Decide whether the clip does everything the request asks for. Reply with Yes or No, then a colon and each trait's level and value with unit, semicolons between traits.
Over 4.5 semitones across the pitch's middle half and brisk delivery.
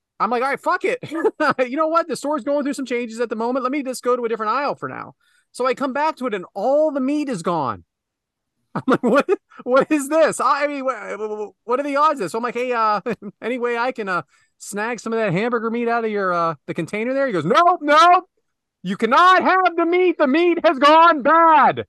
Yes: wide, 5.6 semitones; fast, 255 wpm